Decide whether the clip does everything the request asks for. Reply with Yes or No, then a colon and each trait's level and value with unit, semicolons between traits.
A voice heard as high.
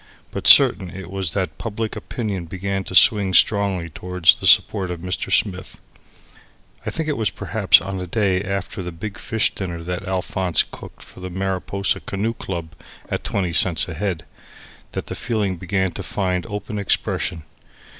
No: very low, 95 Hz